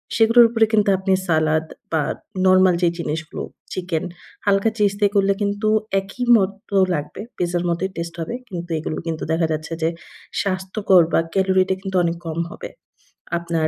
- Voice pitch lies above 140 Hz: Yes, medium, 185 Hz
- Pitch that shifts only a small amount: No, average, 3.1 semitones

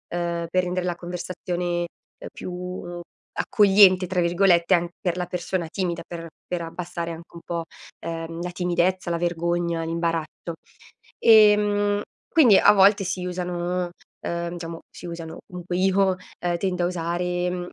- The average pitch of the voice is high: No, medium, 175 Hz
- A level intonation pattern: Yes, narrow, 1.3 semitones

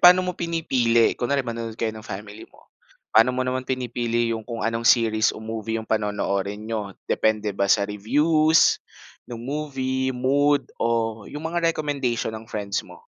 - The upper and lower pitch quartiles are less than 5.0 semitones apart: Yes, average, 3.5 semitones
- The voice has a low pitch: Yes, low, 115 Hz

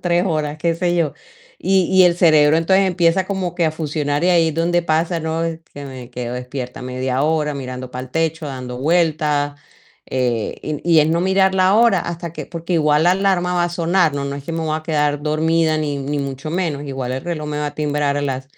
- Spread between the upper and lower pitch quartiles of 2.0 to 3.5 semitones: Yes, average, 3.2 semitones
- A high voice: No, medium, 155 Hz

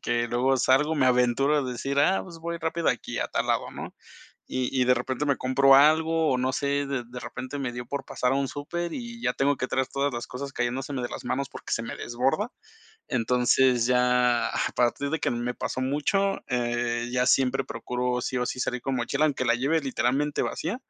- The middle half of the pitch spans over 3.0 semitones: No, narrow, 2.6 semitones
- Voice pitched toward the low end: Yes, low, 130 Hz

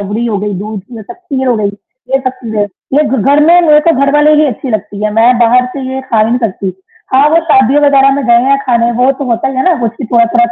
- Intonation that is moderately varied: Yes, average, 3.6 semitones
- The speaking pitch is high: Yes, very high, 250 Hz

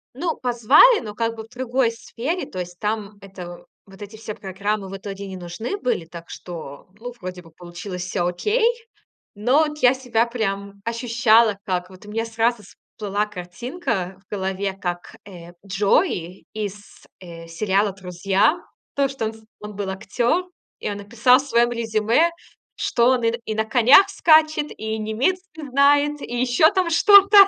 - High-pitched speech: Yes, high, 220 Hz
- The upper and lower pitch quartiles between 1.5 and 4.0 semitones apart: No, average, 4.6 semitones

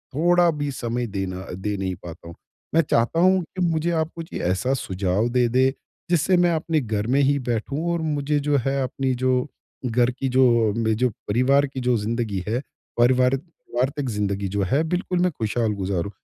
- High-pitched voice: No, low, 125 Hz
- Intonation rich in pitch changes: Yes, wide, 6.0 semitones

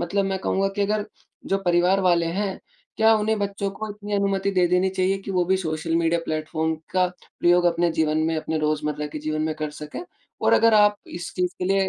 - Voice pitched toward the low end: No, medium, 180 Hz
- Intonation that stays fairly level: No, average, 3.6 semitones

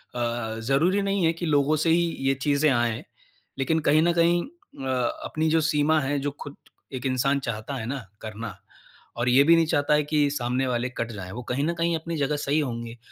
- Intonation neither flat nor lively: Yes, average, 4.4 semitones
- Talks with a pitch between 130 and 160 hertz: Yes, medium, 140 Hz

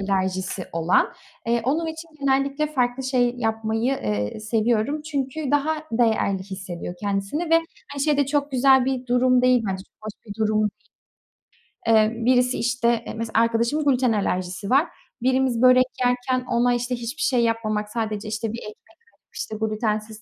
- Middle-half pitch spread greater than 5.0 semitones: No, average, 3.5 semitones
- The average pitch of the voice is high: Yes, high, 235 Hz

